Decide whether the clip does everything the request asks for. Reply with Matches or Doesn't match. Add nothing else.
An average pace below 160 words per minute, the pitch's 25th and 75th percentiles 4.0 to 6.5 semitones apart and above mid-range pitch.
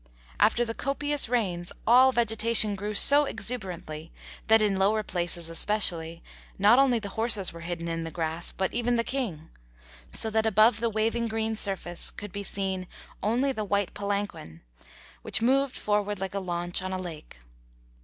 Doesn't match